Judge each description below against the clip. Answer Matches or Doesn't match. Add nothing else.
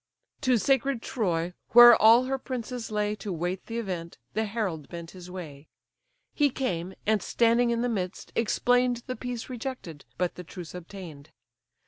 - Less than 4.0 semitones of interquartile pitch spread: Doesn't match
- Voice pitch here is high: Matches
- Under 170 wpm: Matches